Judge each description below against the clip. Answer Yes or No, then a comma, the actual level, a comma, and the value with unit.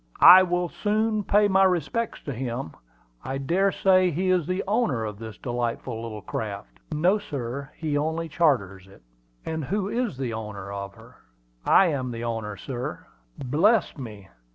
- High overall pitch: No, medium, 140 Hz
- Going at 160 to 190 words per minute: Yes, average, 165 wpm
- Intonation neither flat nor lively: No, wide, 8.4 semitones